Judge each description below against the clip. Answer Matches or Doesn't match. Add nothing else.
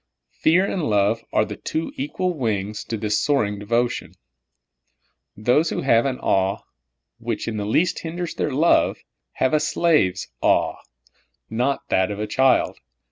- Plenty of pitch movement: Matches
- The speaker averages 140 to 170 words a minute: Matches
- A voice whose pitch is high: Doesn't match